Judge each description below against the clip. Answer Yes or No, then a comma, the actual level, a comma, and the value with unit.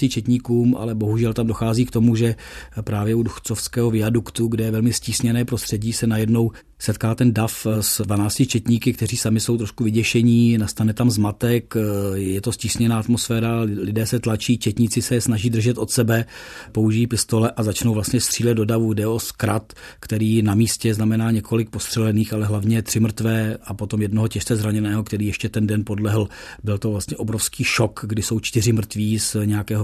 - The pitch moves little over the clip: Yes, narrow, 1.5 semitones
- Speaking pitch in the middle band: No, low, 110 Hz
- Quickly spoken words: Yes, fast, 180 wpm